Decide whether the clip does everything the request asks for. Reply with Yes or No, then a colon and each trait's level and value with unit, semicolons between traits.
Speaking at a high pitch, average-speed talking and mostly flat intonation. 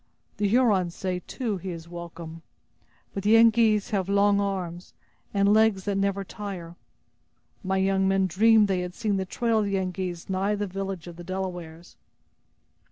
Yes: high, 195 Hz; average, 165 wpm; narrow, 2.3 semitones